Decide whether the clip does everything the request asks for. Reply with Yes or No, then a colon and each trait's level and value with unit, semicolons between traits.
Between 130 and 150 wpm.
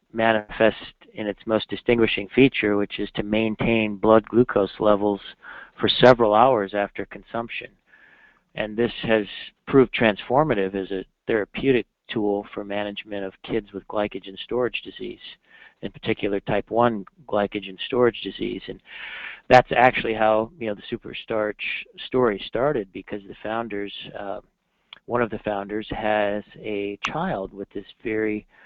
Yes: average, 140 wpm